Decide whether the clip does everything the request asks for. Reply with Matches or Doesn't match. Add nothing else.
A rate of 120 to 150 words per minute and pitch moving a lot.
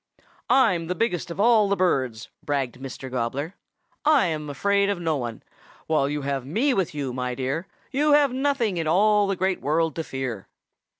Doesn't match